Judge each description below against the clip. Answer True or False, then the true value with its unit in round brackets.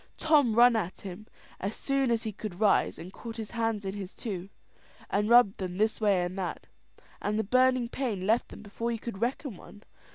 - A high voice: True (220 Hz)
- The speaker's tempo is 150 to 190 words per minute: False (205 wpm)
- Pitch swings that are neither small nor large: True (3.3 semitones)